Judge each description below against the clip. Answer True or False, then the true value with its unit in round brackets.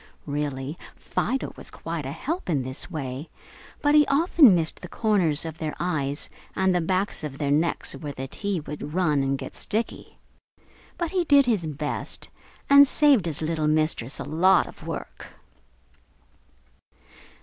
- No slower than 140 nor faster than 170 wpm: True (160 wpm)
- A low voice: False (165 Hz)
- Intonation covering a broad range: True (6.3 semitones)